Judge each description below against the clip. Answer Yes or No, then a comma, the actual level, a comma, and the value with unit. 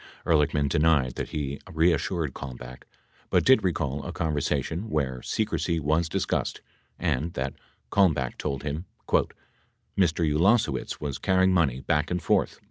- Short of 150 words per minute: Yes, average, 140 wpm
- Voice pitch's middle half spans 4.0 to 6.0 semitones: No, average, 3.4 semitones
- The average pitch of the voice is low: Yes, very low, 75 Hz